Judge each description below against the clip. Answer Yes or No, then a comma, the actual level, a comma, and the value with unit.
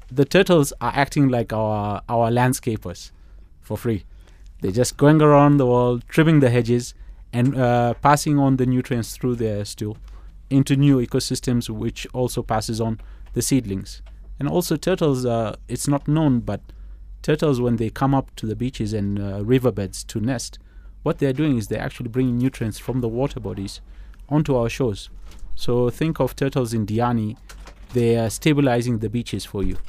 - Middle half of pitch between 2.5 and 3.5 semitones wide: No, average, 4.5 semitones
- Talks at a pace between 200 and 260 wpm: No, average, 170 wpm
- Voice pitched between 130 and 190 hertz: No, low, 120 Hz